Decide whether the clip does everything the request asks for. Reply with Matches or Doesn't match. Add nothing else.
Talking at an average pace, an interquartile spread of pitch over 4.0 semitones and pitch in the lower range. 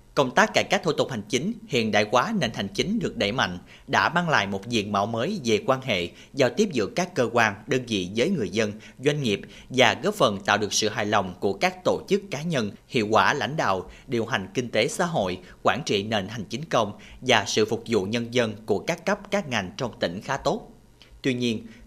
Matches